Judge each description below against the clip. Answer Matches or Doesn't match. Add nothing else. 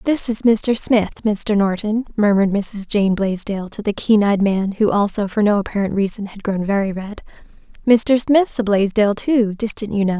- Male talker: Doesn't match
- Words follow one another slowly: Doesn't match